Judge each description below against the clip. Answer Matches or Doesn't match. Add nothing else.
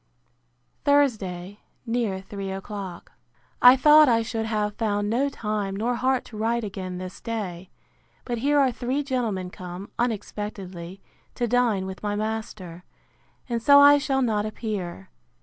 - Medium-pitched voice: Doesn't match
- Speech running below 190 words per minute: Matches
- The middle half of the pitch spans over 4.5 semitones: Doesn't match